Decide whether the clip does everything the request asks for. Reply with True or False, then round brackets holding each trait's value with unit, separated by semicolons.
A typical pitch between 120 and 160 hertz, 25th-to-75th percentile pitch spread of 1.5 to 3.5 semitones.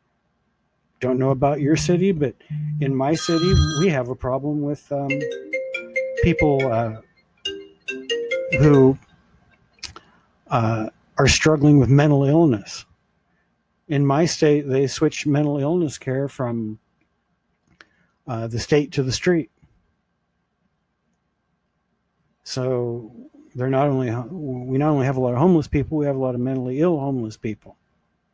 False (140 Hz; 3.9 semitones)